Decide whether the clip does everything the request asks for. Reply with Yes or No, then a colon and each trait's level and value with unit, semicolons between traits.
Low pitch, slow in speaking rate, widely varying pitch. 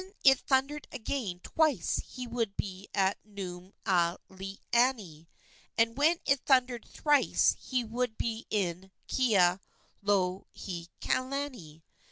No: high, 220 Hz; slow, 100 wpm; wide, 5.7 semitones